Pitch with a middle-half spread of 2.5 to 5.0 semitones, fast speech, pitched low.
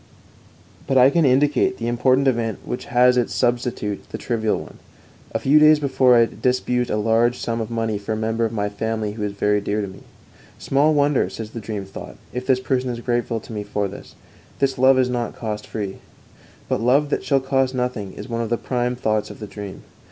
Yes: average, 3.1 semitones; fast, 225 wpm; low, 120 Hz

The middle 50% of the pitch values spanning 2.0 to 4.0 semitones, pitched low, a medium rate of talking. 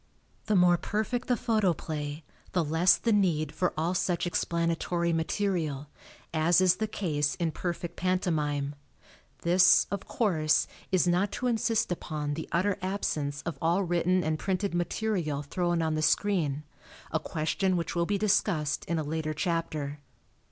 No: average, 3.2 semitones; medium, 170 Hz; average, 150 wpm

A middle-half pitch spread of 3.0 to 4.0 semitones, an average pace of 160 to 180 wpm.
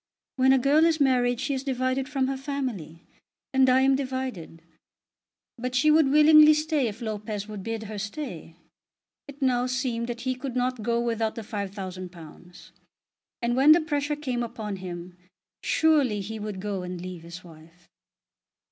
No: average, 5.1 semitones; average, 165 wpm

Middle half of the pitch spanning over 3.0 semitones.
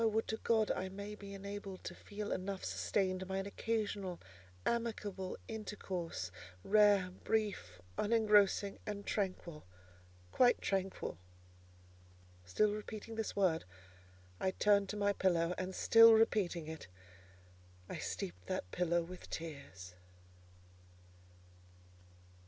No: narrow, 2.6 semitones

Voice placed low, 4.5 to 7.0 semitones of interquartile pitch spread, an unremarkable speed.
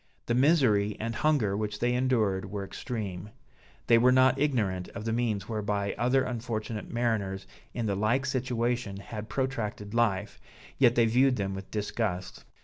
No: low, 110 Hz; average, 3.3 semitones; average, 155 wpm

